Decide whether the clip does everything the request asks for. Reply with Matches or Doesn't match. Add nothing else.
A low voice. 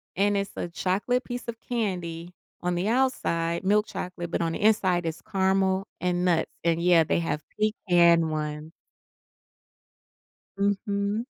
Doesn't match